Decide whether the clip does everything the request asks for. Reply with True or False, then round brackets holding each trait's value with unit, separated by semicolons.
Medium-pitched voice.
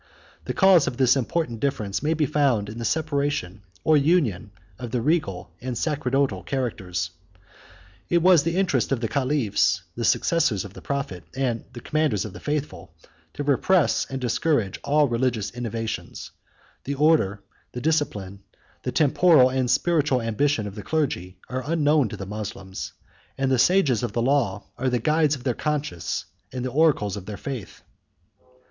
False (130 Hz)